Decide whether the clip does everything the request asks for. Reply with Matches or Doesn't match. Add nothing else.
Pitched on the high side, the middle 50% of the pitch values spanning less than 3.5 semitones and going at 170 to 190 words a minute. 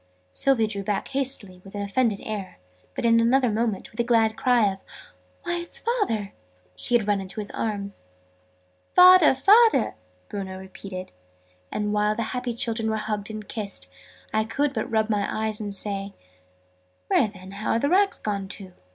Matches